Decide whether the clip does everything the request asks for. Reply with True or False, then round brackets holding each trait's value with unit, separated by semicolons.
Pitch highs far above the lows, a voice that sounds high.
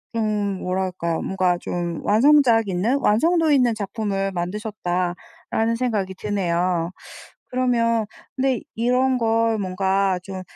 False (3.9 semitones; 210 Hz)